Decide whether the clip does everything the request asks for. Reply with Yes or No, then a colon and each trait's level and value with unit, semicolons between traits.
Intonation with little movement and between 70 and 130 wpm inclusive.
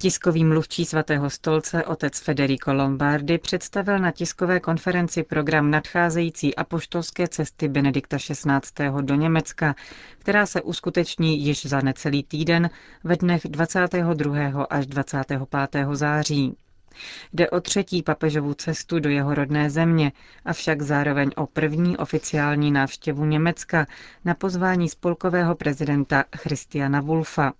No: average, 3.0 semitones; average, 120 wpm